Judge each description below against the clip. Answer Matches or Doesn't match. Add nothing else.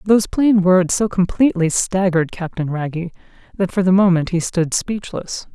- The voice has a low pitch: Doesn't match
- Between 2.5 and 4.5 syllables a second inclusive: Doesn't match